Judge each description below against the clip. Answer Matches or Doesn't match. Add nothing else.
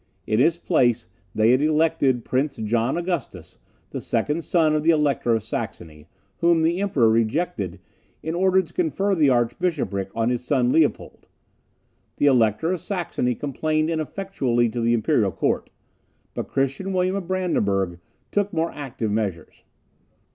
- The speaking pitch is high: Doesn't match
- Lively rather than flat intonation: Matches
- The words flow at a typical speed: Matches